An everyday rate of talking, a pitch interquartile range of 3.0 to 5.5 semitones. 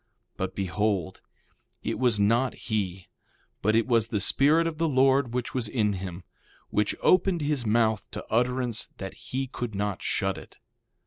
Yes: average, 165 wpm; average, 4.2 semitones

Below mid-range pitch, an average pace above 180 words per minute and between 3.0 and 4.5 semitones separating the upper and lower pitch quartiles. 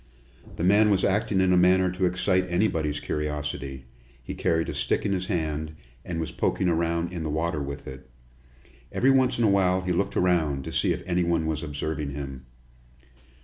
Yes: very low, 85 Hz; average, 190 wpm; average, 3.6 semitones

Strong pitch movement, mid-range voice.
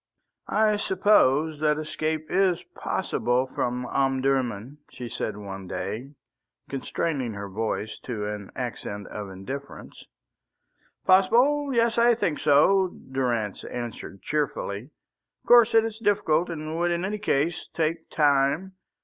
Yes: wide, 7.5 semitones; medium, 145 Hz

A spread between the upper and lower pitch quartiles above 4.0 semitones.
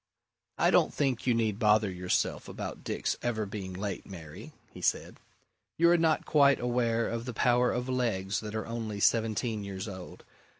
No: average, 3.4 semitones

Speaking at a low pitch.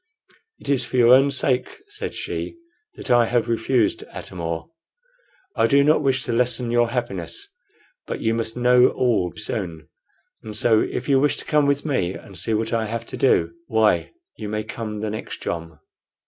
Yes: low, 120 Hz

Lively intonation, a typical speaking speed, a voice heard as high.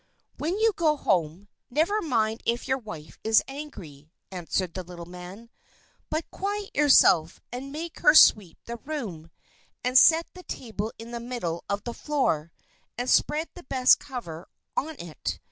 Yes: wide, 8.9 semitones; average, 160 wpm; high, 235 Hz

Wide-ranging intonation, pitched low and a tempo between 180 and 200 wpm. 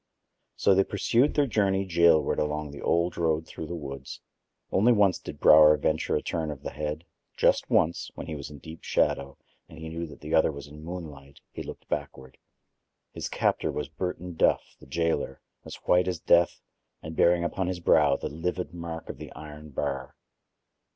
No: average, 2.8 semitones; very low, 80 Hz; average, 190 wpm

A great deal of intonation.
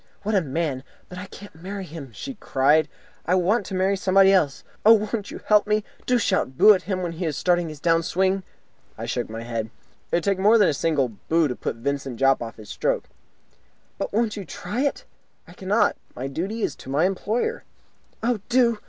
Yes: wide, 5.9 semitones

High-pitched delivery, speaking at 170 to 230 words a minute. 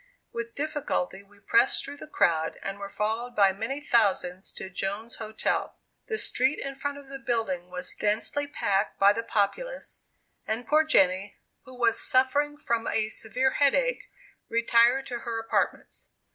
No: high, 230 Hz; average, 160 wpm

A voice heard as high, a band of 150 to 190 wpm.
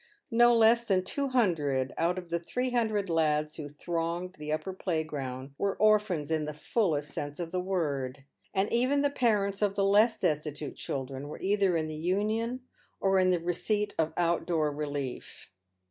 No: medium, 175 Hz; average, 180 wpm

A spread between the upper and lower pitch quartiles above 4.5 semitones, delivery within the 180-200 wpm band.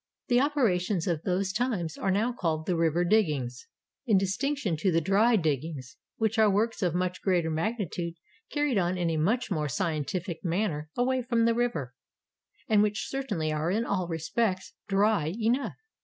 No: average, 5.3 semitones; average, 170 wpm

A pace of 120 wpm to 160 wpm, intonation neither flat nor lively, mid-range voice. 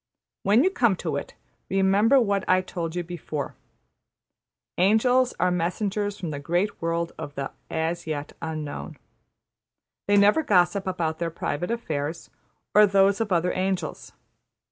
Yes: average, 145 wpm; average, 3.5 semitones; medium, 180 Hz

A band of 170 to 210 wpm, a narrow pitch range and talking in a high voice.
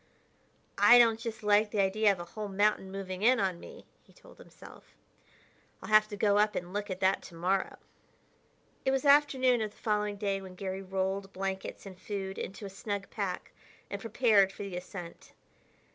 Yes: average, 190 wpm; narrow, 1.9 semitones; high, 200 Hz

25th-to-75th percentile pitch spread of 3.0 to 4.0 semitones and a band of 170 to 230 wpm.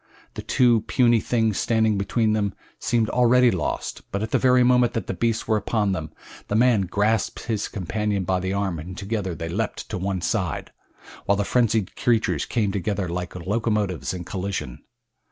Yes: average, 3.3 semitones; average, 180 wpm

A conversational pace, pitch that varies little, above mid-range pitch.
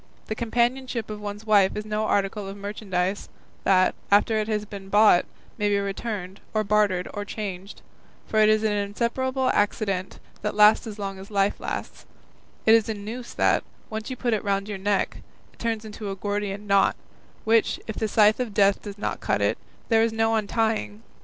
Yes: average, 190 wpm; narrow, 1.7 semitones; high, 210 Hz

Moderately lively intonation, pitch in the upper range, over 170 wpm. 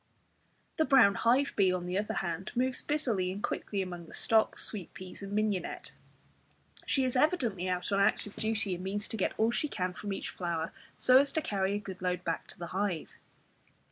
Yes: average, 3.8 semitones; high, 200 Hz; fast, 205 wpm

